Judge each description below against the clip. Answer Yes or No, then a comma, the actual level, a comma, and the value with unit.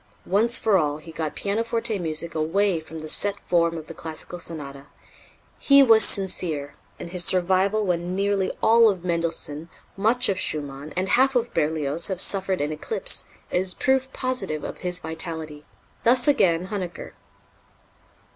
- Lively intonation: No, average, 4.4 semitones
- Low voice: No, medium, 180 Hz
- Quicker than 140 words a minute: Yes, average, 155 wpm